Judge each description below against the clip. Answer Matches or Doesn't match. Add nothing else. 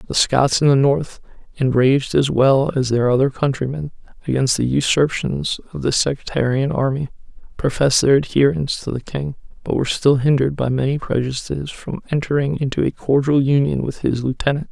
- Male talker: Matches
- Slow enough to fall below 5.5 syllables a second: Doesn't match